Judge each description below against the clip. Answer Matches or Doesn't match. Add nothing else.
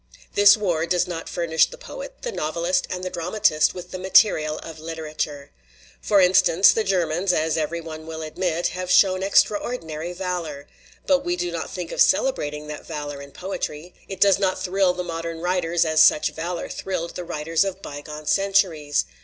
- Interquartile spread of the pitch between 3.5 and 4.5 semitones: Doesn't match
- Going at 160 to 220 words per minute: Matches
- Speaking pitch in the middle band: Matches